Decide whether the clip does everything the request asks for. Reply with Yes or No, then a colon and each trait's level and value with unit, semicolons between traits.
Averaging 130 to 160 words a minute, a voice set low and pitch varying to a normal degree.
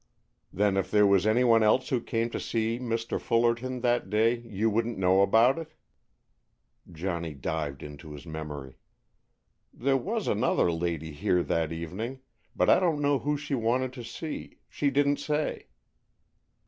No: average, 155 wpm; low, 115 Hz; wide, 6.6 semitones